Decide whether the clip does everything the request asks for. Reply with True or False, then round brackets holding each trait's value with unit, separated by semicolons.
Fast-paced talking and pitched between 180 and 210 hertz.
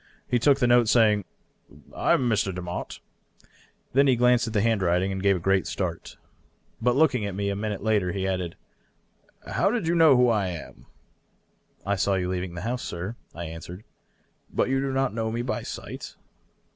False (210 wpm; 105 Hz)